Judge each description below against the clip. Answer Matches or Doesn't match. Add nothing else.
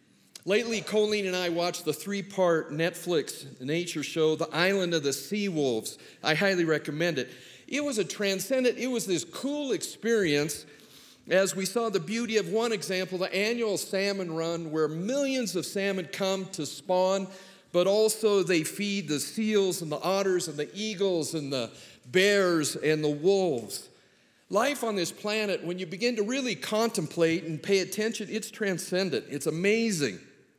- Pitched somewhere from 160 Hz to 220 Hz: Matches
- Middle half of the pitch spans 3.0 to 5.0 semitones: Matches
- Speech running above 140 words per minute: Matches